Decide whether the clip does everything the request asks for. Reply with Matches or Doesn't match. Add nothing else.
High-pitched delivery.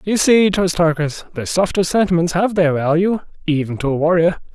Doesn't match